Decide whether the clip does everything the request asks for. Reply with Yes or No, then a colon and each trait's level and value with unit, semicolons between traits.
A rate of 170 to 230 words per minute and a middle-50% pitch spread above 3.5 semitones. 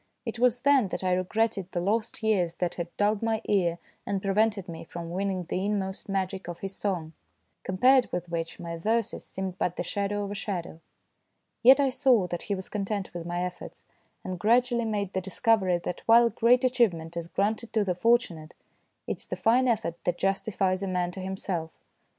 Yes: average, 195 wpm; average, 3.9 semitones